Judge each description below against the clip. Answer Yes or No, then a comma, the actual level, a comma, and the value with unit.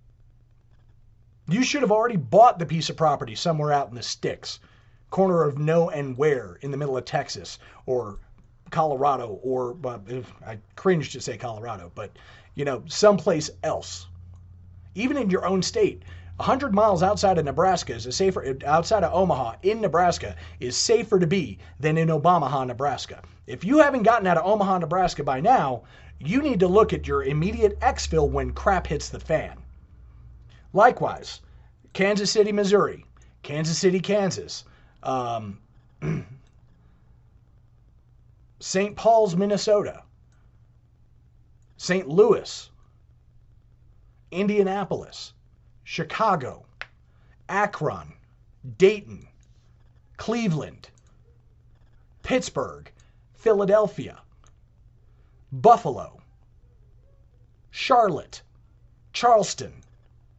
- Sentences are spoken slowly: Yes, slow, 110 wpm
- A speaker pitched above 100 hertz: Yes, medium, 140 Hz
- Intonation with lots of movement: Yes, wide, 8.7 semitones